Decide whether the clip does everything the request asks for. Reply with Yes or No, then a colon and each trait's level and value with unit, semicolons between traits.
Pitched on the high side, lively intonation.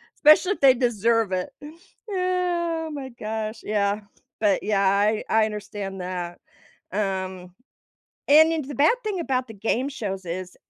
Yes: high, 220 Hz; wide, 6.8 semitones